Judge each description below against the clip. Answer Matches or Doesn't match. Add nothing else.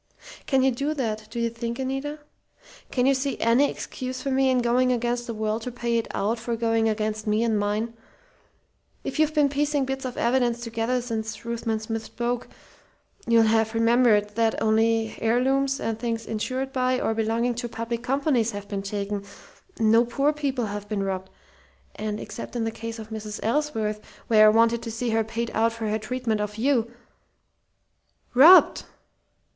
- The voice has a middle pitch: Doesn't match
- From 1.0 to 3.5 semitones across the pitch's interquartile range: Matches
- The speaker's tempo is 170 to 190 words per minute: Matches